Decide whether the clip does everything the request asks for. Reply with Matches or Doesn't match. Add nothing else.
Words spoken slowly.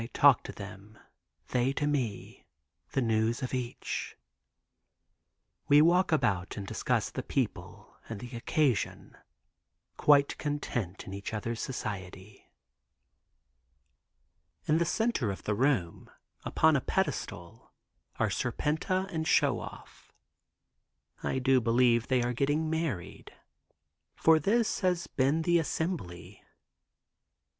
Matches